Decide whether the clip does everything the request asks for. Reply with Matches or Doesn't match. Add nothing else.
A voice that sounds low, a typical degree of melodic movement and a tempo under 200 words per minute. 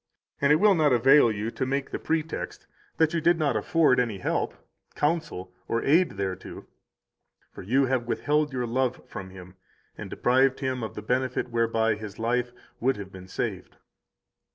Matches